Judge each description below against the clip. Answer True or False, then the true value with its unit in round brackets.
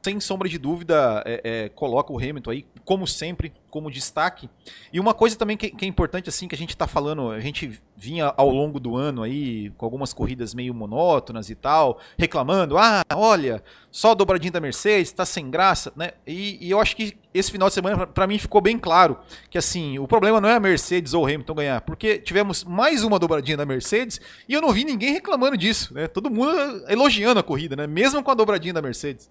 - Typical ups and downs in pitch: False (6.7 semitones)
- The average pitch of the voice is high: False (175 Hz)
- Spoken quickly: True (220 wpm)